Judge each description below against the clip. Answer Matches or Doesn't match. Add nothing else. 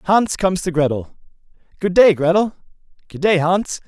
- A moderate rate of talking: Matches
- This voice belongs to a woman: Doesn't match